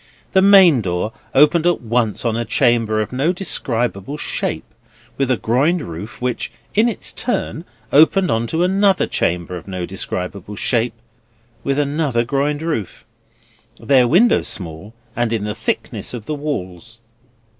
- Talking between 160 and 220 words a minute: No, average, 145 wpm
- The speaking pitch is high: No, low, 125 Hz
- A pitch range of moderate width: No, wide, 6.2 semitones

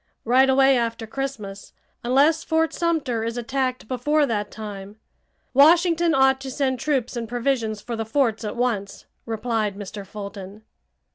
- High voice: Yes, high, 245 Hz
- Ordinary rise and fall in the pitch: Yes, average, 4.0 semitones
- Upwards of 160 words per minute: No, average, 145 wpm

